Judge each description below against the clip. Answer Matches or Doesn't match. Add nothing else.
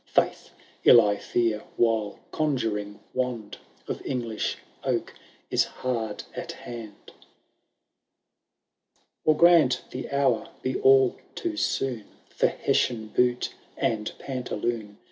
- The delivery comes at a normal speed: Doesn't match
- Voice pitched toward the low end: Matches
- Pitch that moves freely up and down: Doesn't match